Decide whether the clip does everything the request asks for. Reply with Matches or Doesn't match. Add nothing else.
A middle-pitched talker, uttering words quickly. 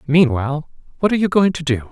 Matches